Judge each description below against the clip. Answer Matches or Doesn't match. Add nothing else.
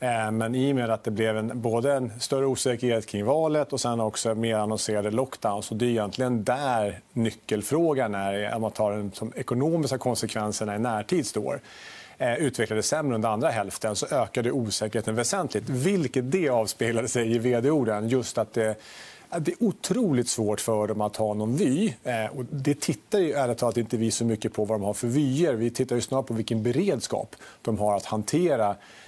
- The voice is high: Doesn't match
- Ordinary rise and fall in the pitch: Matches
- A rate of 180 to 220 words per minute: Matches